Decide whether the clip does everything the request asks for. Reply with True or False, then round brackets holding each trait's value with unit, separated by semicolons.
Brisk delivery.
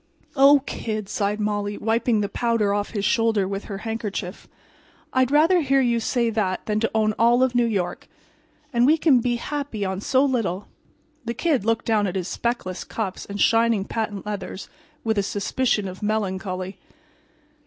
False (175 wpm)